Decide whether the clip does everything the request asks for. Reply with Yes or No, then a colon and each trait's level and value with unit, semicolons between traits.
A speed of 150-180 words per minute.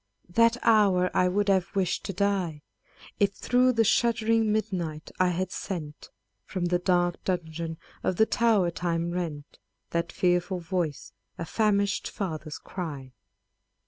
No: average, 140 wpm